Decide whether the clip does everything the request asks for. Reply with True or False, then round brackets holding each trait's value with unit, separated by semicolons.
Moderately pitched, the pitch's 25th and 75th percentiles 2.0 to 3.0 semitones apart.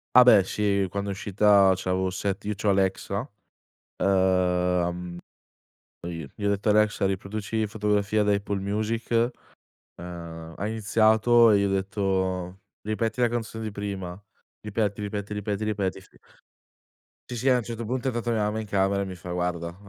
False (100 Hz; 2.4 semitones)